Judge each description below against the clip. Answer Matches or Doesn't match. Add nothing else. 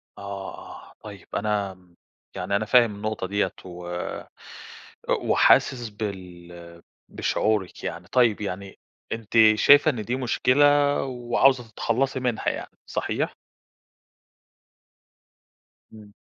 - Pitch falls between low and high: Doesn't match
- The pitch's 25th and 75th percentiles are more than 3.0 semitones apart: Matches